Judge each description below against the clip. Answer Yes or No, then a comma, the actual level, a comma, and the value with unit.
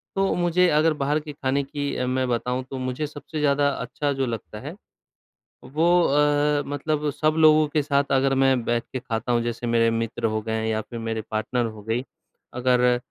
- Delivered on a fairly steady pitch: No, average, 3.6 semitones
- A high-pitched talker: No, low, 135 Hz